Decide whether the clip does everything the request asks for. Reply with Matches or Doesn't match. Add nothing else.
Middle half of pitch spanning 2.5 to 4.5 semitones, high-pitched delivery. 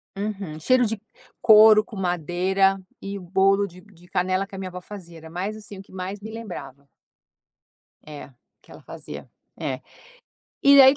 Matches